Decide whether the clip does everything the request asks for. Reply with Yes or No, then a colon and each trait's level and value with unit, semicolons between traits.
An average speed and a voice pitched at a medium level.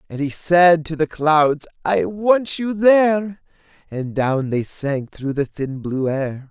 Yes: average, 175 wpm; medium, 160 Hz